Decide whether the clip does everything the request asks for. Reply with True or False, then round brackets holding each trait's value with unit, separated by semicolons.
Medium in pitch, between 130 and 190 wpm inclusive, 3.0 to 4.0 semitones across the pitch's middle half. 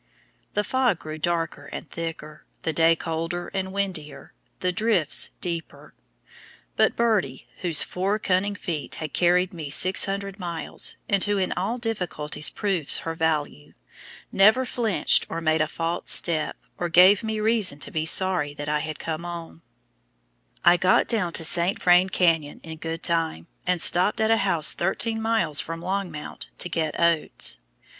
True (175 Hz; 160 wpm; 3.5 semitones)